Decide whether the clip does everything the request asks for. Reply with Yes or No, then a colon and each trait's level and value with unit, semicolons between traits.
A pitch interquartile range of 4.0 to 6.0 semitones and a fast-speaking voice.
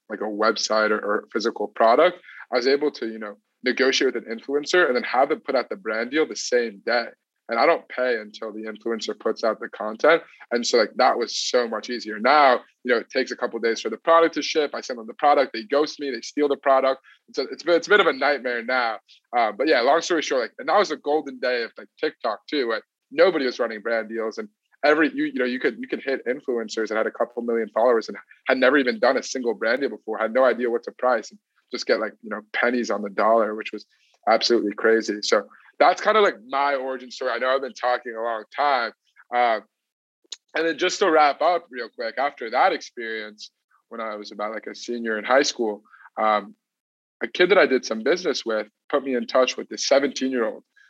Yes: average, 4.3 semitones; fast, 245 wpm